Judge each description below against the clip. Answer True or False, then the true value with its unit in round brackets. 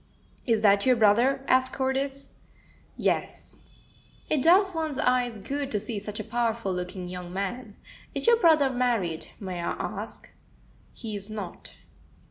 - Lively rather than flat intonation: False (5.0 semitones)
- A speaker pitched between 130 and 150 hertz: False (235 Hz)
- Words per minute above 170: False (145 wpm)